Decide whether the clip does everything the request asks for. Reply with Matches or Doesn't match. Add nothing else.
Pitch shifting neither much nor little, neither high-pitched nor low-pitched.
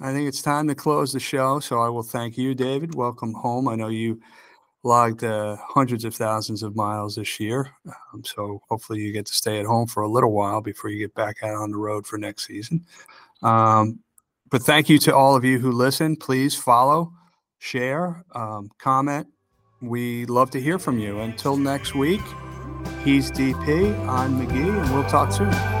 Doesn't match